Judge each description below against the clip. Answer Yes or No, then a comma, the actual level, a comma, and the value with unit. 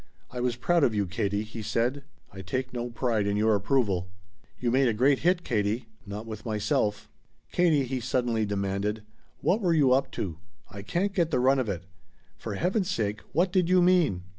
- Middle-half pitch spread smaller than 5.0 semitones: No, wide, 5.4 semitones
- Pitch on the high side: No, low, 120 Hz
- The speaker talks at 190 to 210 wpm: Yes, average, 195 wpm